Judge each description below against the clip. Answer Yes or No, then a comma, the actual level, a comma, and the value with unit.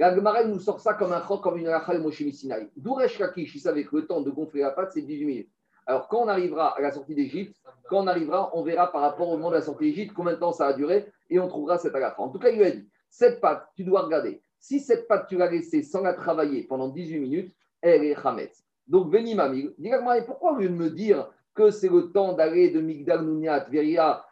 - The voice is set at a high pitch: No, medium, 180 Hz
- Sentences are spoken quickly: Yes, fast, 250 wpm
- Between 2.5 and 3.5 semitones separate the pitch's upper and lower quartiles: No, average, 5.0 semitones